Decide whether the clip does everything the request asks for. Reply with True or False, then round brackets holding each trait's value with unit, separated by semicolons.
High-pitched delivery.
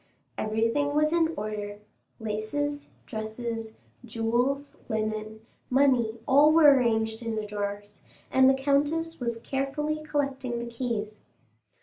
True (235 Hz)